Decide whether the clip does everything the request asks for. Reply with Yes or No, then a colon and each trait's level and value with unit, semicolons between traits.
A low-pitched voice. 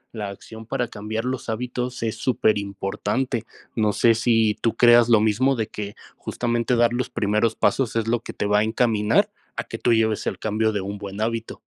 Yes: low, 110 Hz